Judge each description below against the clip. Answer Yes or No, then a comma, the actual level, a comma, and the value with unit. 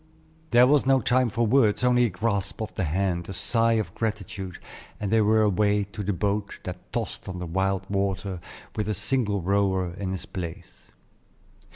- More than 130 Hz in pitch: No, low, 100 Hz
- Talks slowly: No, average, 185 wpm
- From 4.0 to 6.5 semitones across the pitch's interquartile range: No, average, 2.8 semitones